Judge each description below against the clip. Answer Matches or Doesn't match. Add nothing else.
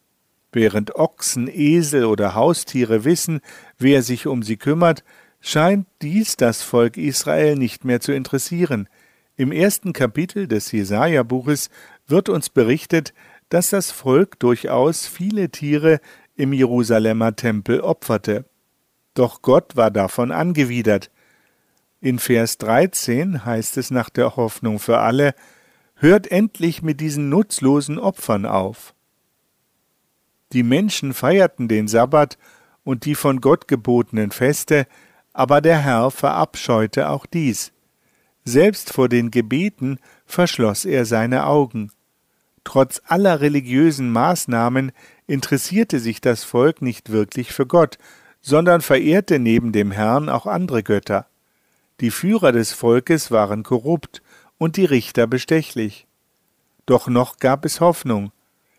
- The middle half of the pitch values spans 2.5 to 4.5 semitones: Doesn't match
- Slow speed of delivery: Matches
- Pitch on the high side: Doesn't match